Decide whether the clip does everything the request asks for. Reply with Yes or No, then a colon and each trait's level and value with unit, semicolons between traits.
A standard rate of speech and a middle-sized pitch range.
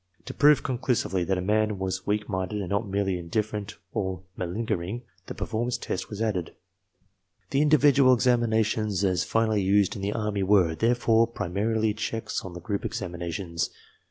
Yes: average, 160 wpm; average, 3.2 semitones